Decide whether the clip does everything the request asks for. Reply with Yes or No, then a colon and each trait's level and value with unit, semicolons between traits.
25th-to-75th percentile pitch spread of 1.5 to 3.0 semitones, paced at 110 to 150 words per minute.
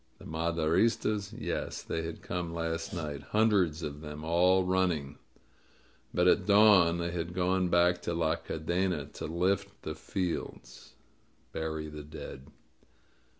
Yes: average, 2.7 semitones; average, 145 wpm